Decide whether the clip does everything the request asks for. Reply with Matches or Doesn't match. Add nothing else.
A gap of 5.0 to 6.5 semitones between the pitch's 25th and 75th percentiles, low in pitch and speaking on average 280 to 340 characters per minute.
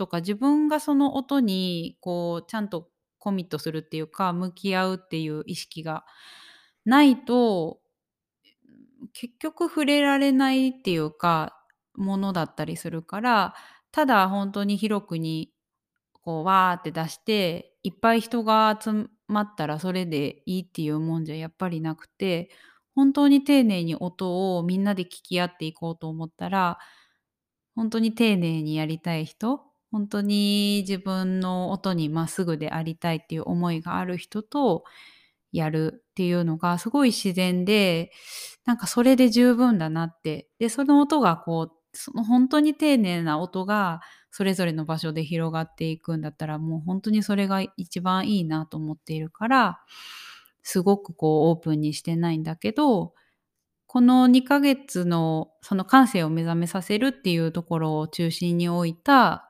Doesn't match